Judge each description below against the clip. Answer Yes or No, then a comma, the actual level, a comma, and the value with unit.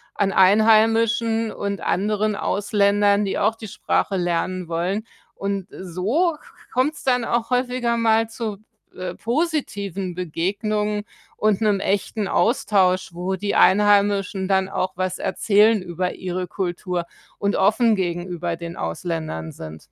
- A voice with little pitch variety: No, average, 3.1 semitones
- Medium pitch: No, high, 200 Hz